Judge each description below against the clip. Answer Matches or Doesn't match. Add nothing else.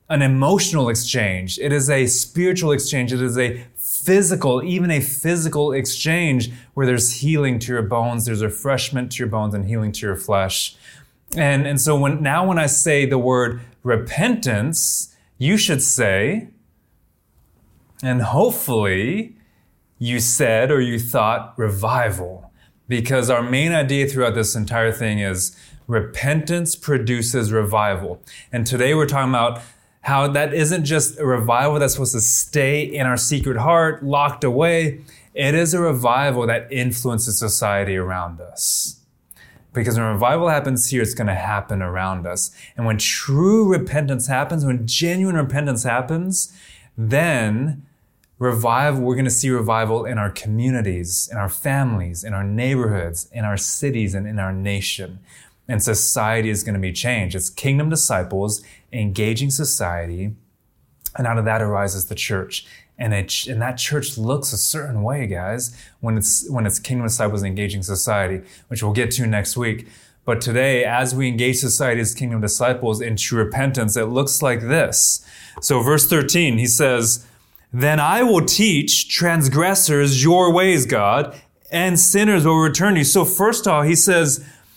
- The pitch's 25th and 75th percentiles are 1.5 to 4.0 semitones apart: Doesn't match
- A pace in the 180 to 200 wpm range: Doesn't match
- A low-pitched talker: Matches